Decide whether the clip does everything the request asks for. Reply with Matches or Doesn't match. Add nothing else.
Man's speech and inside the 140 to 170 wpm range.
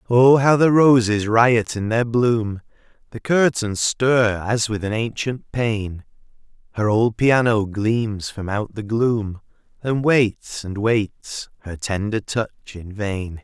Matches